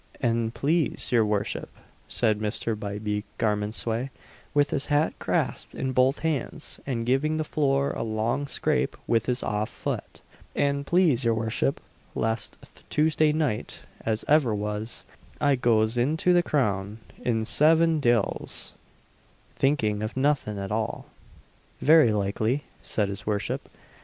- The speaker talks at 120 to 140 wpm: Yes, slow, 135 wpm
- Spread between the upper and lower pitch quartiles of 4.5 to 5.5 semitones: Yes, average, 5.1 semitones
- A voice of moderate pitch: No, low, 120 Hz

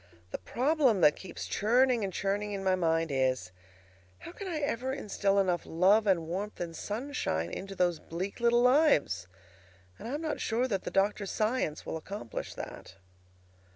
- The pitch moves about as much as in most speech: No, wide, 6.2 semitones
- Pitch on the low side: No, high, 200 Hz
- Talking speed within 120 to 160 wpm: No, average, 170 wpm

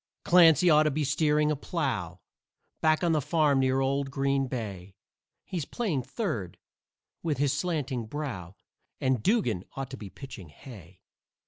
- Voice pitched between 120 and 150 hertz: Yes, low, 135 Hz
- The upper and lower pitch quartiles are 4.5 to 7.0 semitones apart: Yes, average, 5.0 semitones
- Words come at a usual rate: Yes, average, 150 wpm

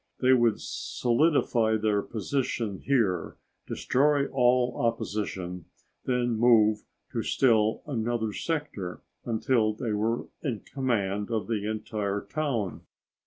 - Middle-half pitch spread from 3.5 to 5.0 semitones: No, average, 3.0 semitones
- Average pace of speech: No, slow, 110 wpm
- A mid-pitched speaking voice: No, low, 115 Hz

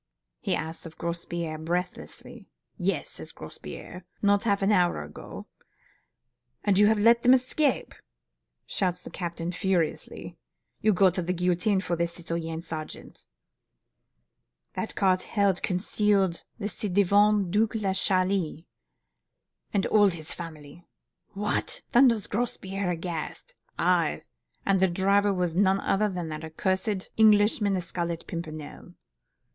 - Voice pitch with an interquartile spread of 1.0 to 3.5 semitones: Yes, average, 3.2 semitones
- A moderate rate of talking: No, slow, 130 wpm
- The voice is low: No, medium, 185 Hz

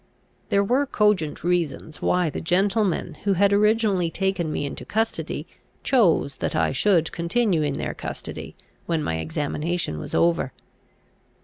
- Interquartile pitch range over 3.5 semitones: Yes, average, 4.6 semitones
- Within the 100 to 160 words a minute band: Yes, average, 140 wpm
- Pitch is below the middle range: No, medium, 175 Hz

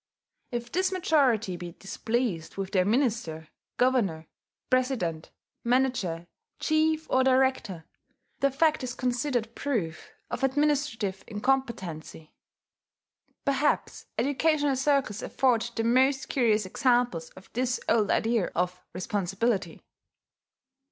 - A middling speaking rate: No, slow, 105 wpm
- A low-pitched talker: No, high, 240 Hz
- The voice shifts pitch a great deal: Yes, wide, 5.7 semitones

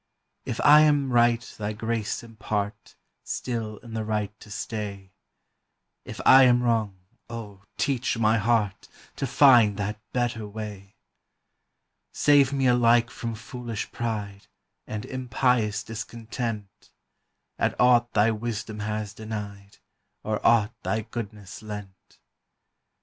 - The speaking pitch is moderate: No, low, 110 Hz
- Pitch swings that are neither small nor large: No, narrow, 2.3 semitones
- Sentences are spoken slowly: Yes, slow, 120 wpm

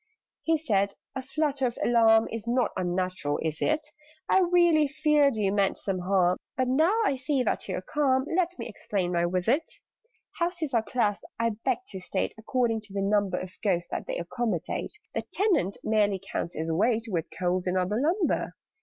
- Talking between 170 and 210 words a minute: Yes, average, 185 wpm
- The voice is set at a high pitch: Yes, high, 225 Hz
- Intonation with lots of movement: Yes, wide, 7.2 semitones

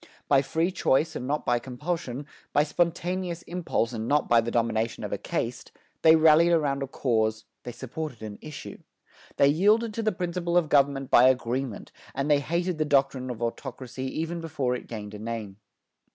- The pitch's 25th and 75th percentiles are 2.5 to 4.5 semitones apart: No, wide, 5.5 semitones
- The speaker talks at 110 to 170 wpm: No, average, 180 wpm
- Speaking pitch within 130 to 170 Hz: Yes, medium, 140 Hz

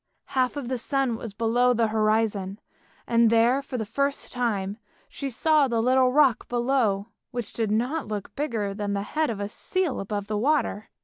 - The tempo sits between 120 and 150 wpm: No, average, 185 wpm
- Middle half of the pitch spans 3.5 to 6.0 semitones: Yes, average, 3.8 semitones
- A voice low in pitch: No, high, 235 Hz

